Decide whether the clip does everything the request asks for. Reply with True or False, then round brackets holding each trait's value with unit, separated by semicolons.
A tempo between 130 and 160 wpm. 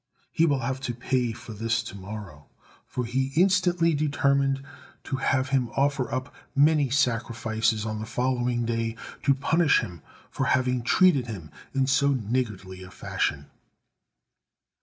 True (145 wpm)